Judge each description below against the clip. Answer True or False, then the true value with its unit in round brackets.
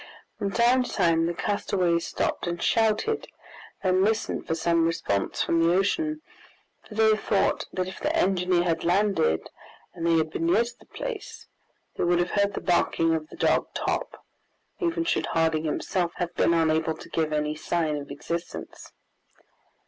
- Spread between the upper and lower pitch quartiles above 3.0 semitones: True (3.8 semitones)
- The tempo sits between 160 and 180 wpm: True (170 wpm)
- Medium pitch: True (175 Hz)